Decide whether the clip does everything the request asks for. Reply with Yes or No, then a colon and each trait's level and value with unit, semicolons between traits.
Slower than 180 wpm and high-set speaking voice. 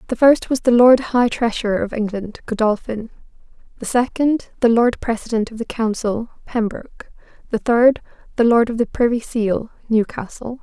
Yes: average, 160 wpm; high, 230 Hz